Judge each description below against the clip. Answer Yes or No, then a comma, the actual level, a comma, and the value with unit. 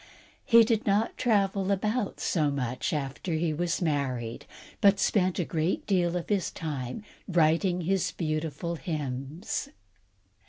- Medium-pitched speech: Yes, medium, 170 Hz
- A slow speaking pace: Yes, slow, 130 wpm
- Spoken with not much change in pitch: No, average, 4.5 semitones